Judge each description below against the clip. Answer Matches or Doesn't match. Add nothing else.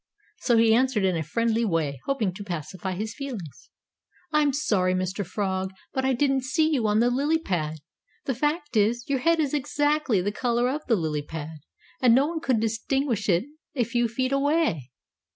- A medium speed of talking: Matches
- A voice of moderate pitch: Doesn't match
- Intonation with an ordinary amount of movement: Doesn't match